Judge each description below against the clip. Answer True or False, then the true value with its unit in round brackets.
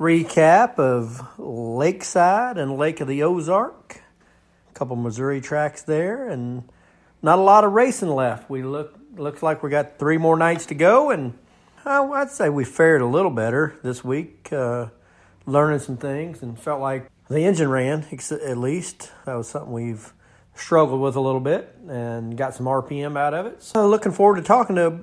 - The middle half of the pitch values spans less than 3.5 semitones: False (4.6 semitones)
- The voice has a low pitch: False (145 Hz)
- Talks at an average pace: True (185 wpm)